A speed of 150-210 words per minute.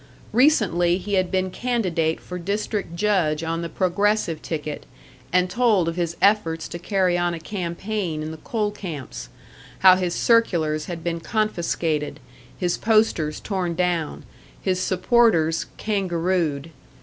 No: slow, 135 wpm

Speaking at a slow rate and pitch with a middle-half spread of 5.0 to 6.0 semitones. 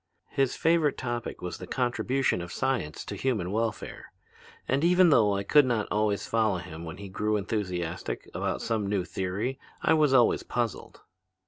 No: average, 165 wpm; wide, 5.5 semitones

